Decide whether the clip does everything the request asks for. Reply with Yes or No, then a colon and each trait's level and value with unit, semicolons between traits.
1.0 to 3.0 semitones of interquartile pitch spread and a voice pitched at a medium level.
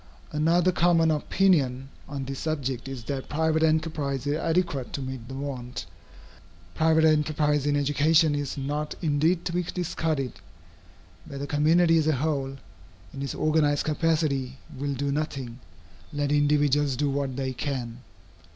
Yes: narrow, 2.6 semitones; medium, 145 Hz